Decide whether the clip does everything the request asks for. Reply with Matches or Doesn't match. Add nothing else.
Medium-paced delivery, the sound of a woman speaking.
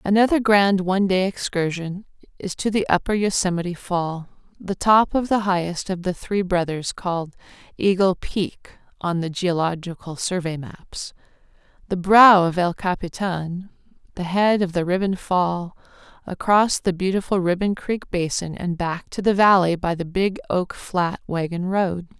Matches